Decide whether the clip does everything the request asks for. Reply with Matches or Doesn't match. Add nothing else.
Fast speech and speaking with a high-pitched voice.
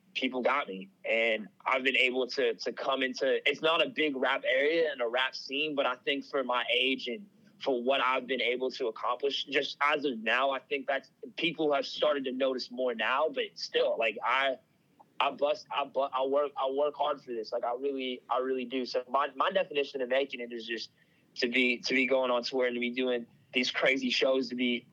Doesn't match